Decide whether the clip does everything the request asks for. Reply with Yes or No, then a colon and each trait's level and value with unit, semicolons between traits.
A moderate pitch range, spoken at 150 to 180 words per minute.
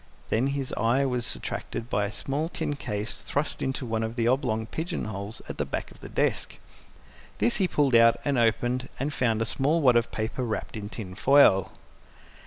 No: average, 3.8 semitones; average, 195 wpm